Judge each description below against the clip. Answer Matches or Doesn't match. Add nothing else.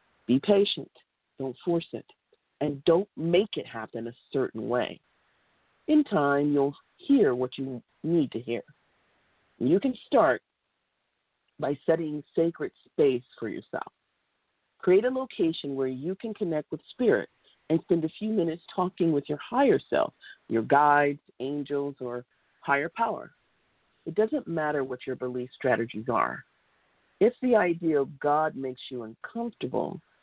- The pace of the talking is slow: Doesn't match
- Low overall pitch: Doesn't match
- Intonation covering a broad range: Matches